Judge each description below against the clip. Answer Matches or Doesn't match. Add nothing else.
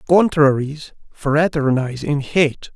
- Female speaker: Doesn't match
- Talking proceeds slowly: Matches